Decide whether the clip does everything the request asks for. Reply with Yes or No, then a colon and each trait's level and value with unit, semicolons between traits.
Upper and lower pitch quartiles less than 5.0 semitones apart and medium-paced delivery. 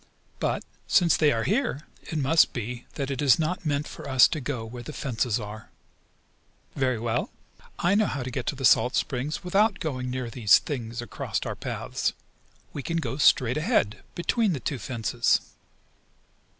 Yes: average, 4.6 semitones; average, 175 wpm